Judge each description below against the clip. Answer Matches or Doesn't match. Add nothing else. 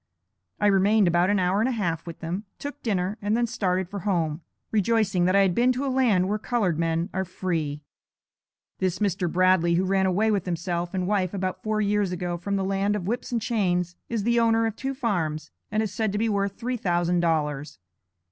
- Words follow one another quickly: Matches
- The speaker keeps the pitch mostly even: Doesn't match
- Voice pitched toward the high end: Matches